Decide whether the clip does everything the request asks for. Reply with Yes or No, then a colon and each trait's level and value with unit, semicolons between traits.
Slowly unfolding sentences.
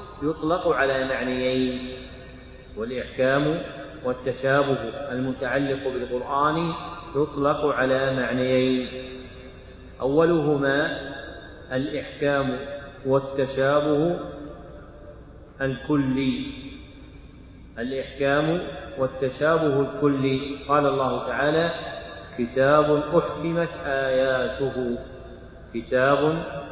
Yes: slow, 55 wpm